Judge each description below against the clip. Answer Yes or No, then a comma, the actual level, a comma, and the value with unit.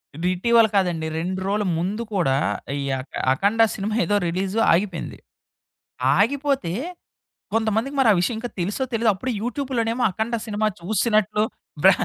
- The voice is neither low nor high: No, high, 210 Hz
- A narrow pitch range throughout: No, average, 3.7 semitones